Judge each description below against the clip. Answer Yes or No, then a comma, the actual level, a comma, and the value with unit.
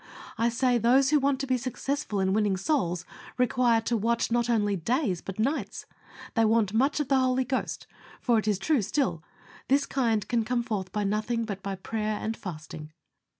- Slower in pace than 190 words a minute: No, average, 195 wpm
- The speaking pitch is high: Yes, high, 230 Hz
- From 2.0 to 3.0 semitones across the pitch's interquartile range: No, average, 3.8 semitones